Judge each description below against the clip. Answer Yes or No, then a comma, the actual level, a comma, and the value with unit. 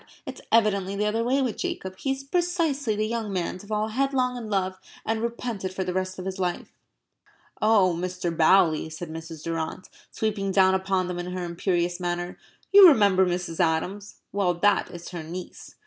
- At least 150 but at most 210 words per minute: Yes, average, 190 wpm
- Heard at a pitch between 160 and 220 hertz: Yes, high, 190 Hz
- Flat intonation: No, average, 3.6 semitones